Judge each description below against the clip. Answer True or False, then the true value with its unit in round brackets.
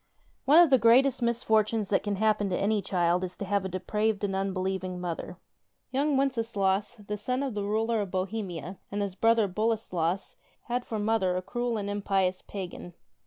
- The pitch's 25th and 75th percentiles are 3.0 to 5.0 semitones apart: True (3.3 semitones)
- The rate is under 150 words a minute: False (180 wpm)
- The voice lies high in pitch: True (205 Hz)